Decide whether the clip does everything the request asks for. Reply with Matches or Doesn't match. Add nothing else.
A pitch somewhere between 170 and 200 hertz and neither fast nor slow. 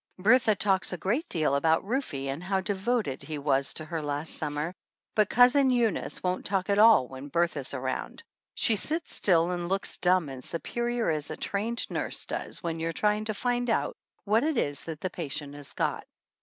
Matches